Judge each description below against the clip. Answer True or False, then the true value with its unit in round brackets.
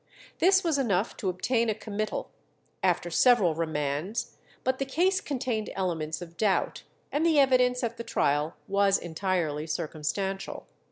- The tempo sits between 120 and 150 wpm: True (145 wpm)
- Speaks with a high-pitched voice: True (200 Hz)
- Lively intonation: True (7.0 semitones)